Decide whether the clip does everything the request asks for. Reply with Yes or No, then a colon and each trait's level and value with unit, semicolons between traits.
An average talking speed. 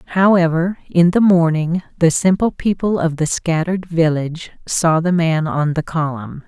Yes: average, 160 wpm